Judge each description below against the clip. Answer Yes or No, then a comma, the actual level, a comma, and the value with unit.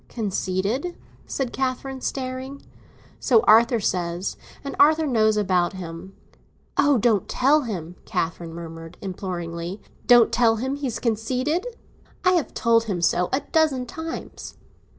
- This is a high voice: Yes, high, 230 Hz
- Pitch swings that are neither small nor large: No, wide, 6.5 semitones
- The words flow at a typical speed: No, slow, 130 wpm